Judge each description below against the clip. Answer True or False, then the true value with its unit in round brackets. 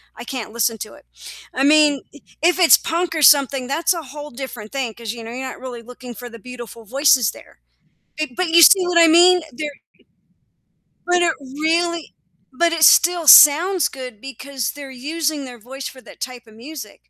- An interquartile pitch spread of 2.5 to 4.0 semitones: False (4.9 semitones)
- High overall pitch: True (275 Hz)